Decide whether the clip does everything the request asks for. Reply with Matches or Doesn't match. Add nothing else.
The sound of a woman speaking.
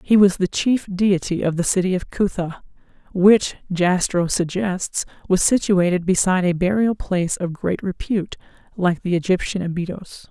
Matches